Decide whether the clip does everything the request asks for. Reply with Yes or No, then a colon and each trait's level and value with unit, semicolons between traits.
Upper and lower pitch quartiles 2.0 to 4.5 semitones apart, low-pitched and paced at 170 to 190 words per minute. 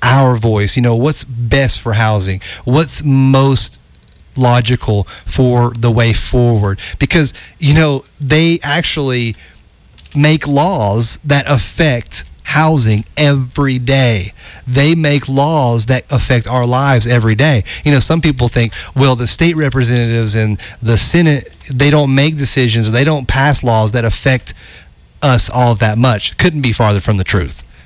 No: average, 4.1 semitones; low, 125 Hz; average, 145 wpm